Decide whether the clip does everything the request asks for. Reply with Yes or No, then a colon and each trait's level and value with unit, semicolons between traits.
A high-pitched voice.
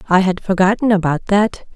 Yes: high, 195 Hz